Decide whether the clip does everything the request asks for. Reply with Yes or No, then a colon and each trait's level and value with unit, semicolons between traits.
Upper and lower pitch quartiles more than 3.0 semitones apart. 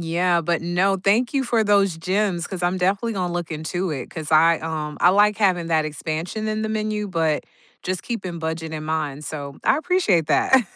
Yes: average, 4.3 semitones